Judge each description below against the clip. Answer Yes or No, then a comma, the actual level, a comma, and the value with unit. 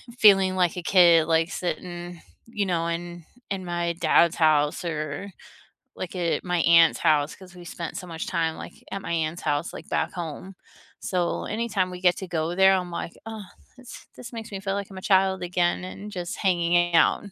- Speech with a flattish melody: Yes, narrow, 2.2 semitones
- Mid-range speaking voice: Yes, medium, 175 Hz